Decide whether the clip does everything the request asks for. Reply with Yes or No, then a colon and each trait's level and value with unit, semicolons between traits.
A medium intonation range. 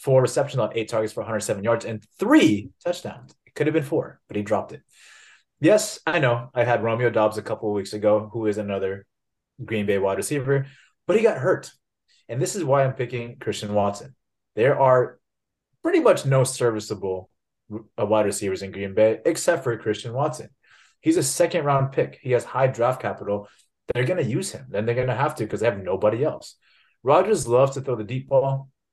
Yes: average, 4.4 semitones